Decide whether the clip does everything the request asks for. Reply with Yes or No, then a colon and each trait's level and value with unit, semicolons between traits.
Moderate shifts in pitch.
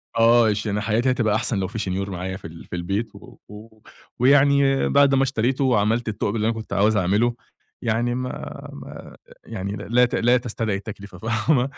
Yes: average, 3.2 semitones